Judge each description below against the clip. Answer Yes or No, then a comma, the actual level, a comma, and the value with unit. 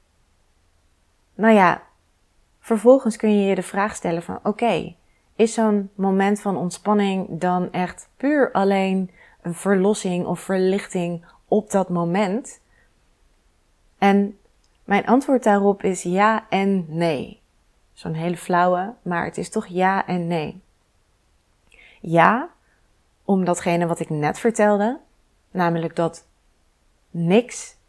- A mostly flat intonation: No, average, 3.5 semitones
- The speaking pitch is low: No, medium, 185 Hz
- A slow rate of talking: Yes, slow, 120 wpm